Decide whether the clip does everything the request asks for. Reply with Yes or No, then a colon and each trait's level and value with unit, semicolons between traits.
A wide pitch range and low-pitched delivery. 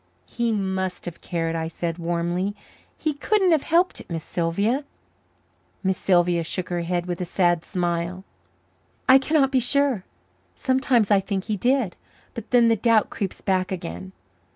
No: wide, 5.7 semitones; high, 190 Hz